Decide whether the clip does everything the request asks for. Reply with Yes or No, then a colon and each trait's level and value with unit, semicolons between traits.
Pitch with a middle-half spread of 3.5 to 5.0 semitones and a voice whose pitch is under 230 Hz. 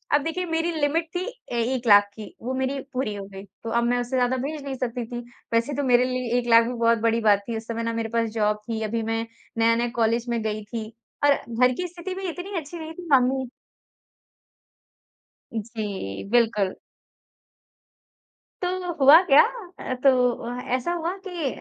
No: average, 4.3 semitones; high, 245 Hz